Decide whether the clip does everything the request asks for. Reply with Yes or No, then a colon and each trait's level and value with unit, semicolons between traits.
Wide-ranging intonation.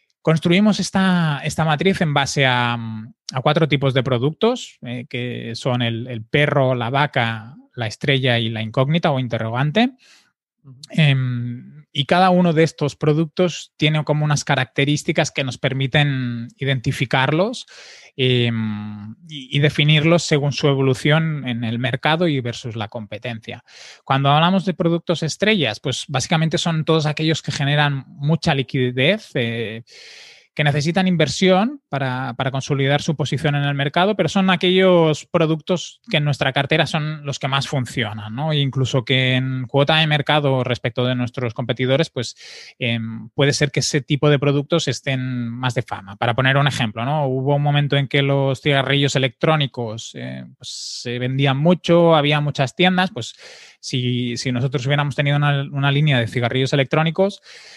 No: average, 3.7 semitones